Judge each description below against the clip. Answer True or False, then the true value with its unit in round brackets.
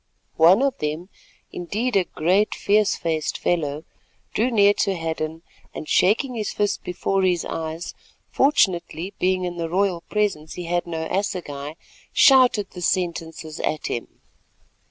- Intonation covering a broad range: False (3.9 semitones)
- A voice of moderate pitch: True (180 Hz)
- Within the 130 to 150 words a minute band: True (135 wpm)